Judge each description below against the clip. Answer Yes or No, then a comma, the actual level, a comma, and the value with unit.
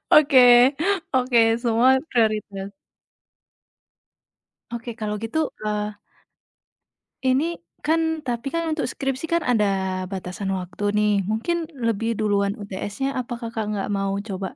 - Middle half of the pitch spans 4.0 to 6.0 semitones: Yes, average, 4.5 semitones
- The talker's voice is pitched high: Yes, high, 225 Hz